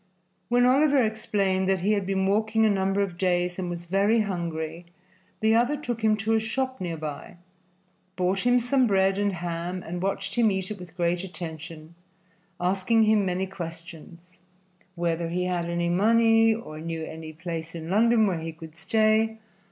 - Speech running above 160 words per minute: Yes, average, 175 wpm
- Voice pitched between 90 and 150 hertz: No, high, 190 Hz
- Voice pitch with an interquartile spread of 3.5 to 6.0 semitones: Yes, average, 4.2 semitones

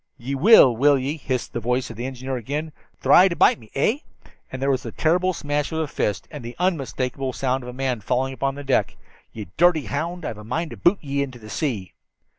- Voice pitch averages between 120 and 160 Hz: Yes, low, 135 Hz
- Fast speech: Yes, fast, 235 wpm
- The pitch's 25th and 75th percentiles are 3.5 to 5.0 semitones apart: Yes, average, 3.9 semitones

